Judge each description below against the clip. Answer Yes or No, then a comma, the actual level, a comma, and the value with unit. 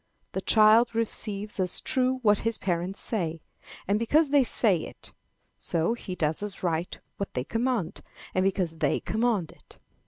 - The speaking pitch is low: No, high, 205 Hz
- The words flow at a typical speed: Yes, average, 160 wpm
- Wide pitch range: No, average, 4.6 semitones